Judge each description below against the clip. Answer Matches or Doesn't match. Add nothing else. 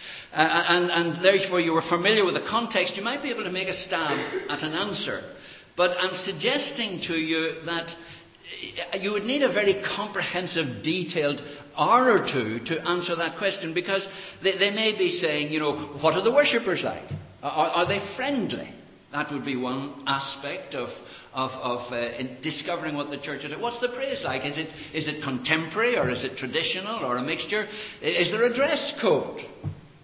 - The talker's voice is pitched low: Doesn't match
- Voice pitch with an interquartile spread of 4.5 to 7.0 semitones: Matches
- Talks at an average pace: Matches